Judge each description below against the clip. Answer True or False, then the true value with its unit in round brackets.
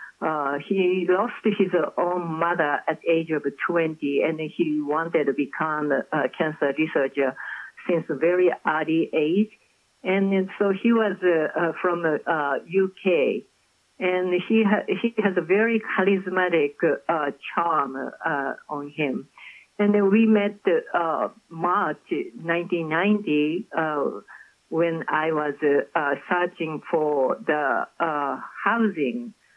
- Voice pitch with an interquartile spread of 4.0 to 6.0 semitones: True (4.3 semitones)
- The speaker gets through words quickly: False (140 wpm)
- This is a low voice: False (175 Hz)